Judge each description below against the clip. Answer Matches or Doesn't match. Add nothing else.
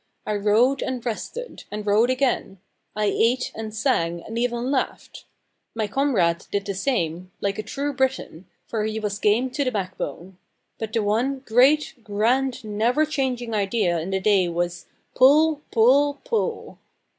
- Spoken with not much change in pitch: Doesn't match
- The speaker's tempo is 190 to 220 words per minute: Doesn't match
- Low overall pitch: Doesn't match